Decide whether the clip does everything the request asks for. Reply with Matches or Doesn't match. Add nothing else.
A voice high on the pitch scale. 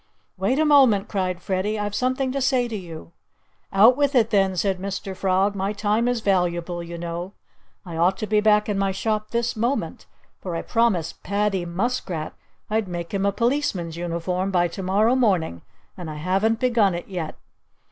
Matches